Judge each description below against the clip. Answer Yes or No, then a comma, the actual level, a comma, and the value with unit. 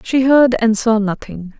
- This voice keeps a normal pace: Yes, average, 190 wpm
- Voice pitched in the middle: No, high, 230 Hz